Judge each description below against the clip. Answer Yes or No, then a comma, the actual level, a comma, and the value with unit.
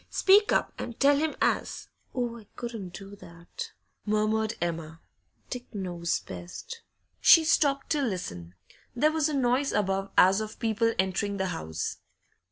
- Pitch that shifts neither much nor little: No, wide, 6.5 semitones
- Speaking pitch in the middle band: No, high, 215 Hz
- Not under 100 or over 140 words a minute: No, average, 155 wpm